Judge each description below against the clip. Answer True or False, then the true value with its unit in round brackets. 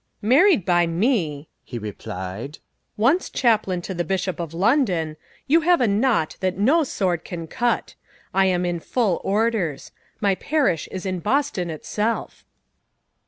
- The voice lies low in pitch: False (190 Hz)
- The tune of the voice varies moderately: False (5.7 semitones)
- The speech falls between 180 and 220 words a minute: False (145 wpm)